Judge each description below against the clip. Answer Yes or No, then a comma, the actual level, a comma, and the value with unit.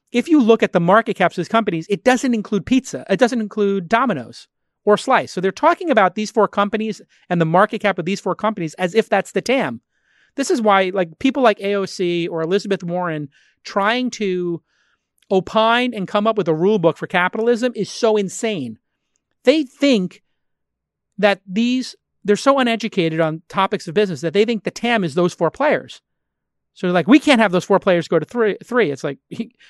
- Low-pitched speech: No, high, 205 Hz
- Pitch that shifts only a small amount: No, average, 4.0 semitones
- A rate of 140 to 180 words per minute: No, average, 200 wpm